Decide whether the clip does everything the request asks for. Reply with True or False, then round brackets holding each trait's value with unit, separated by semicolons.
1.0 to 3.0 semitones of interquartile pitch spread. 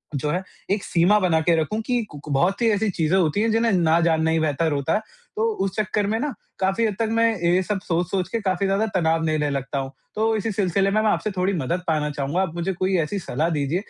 False (4.6 semitones)